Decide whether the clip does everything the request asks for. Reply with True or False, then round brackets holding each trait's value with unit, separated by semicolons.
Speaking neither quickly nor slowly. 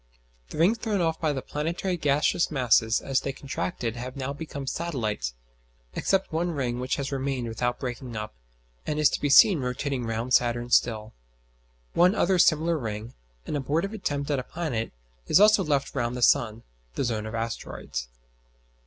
True (170 wpm)